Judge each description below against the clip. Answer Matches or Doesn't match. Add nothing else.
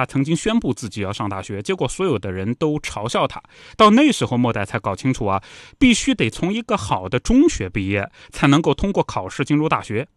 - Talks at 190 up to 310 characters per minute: Doesn't match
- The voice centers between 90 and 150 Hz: Matches